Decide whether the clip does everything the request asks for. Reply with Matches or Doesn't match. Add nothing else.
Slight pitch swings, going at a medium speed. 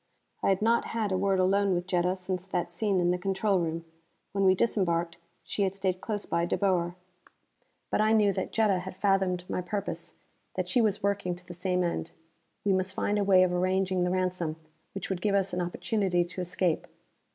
Doesn't match